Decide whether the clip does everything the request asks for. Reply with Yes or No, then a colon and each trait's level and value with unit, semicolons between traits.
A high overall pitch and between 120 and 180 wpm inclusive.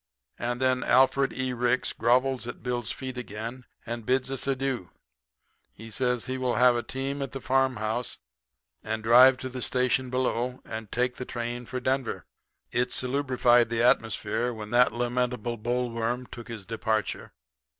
No: low, 125 Hz; average, 160 wpm